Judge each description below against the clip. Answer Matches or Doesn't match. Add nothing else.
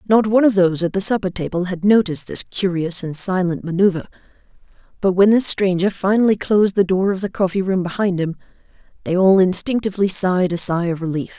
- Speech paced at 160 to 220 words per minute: Matches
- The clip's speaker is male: Doesn't match